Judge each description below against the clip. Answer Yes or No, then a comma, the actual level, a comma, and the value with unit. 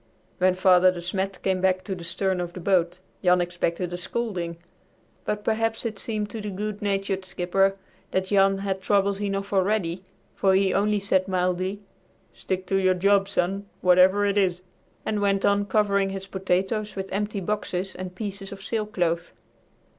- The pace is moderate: Yes, average, 170 wpm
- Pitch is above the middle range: Yes, high, 195 Hz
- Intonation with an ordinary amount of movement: No, narrow, 1.7 semitones